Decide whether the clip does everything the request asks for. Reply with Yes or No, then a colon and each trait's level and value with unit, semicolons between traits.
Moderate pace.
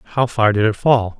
No: fast, 250 wpm